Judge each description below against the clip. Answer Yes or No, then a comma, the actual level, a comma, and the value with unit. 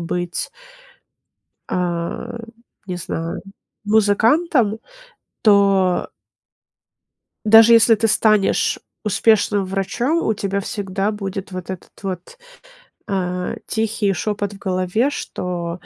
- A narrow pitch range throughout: No, average, 3.1 semitones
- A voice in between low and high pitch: No, high, 200 Hz